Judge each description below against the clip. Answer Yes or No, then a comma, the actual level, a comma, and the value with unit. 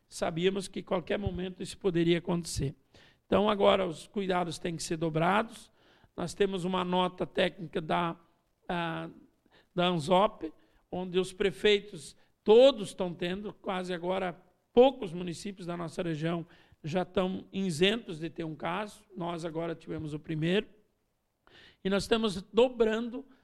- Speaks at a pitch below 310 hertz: Yes, medium, 185 Hz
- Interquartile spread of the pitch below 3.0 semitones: Yes, narrow, 2.6 semitones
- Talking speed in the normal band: Yes, average, 140 wpm